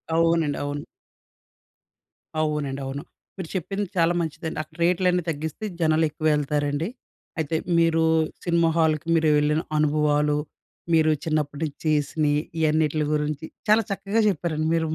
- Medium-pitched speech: Yes, medium, 155 Hz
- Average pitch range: No, narrow, 1.9 semitones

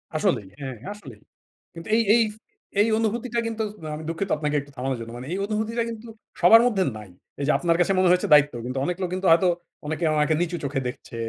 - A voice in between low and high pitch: Yes, medium, 170 Hz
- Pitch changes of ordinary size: No, wide, 7.3 semitones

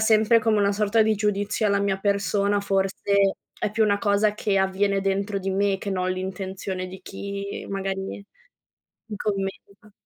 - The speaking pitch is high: Yes, high, 200 Hz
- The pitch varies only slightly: Yes, narrow, 1.2 semitones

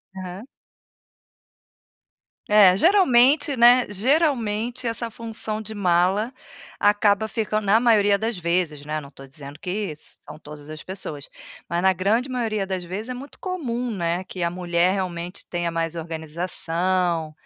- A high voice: Yes, high, 195 Hz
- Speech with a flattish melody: No, average, 5.0 semitones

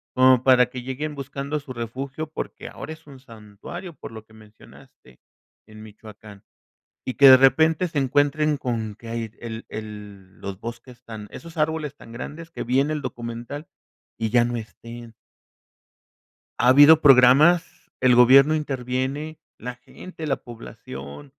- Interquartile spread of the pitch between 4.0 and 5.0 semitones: Yes, average, 4.3 semitones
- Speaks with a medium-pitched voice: No, low, 125 Hz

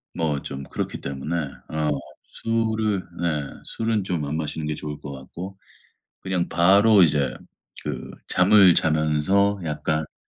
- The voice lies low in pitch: Yes, very low, 80 Hz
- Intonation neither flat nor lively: Yes, average, 4.8 semitones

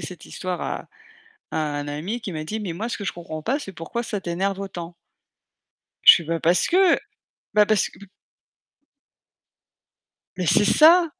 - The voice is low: No, high, 190 Hz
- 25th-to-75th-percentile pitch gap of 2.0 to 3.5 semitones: No, average, 4.8 semitones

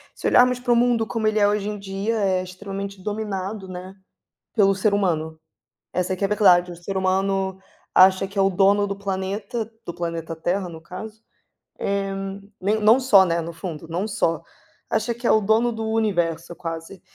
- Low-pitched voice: No, high, 195 Hz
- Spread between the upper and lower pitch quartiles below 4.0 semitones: Yes, average, 2.7 semitones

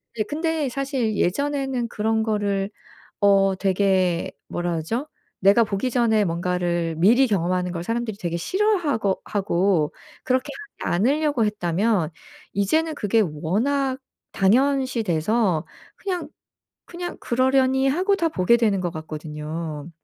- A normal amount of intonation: No, wide, 6.8 semitones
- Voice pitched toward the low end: No, high, 210 Hz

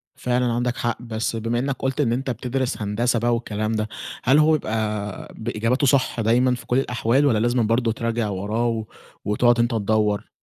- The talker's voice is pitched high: No, low, 115 Hz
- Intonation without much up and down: Yes, narrow, 2.2 semitones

